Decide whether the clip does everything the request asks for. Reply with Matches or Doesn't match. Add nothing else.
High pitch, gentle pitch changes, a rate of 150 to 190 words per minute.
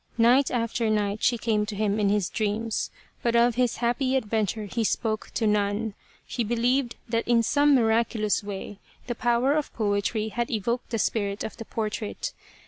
Matches